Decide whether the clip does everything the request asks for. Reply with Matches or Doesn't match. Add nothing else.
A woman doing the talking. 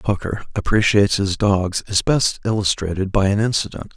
Doesn't match